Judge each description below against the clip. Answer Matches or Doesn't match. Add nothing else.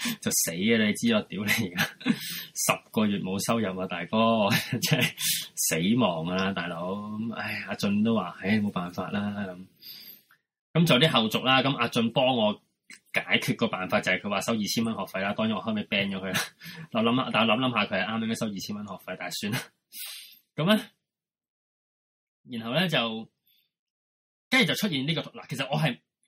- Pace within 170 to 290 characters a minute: Matches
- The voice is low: Matches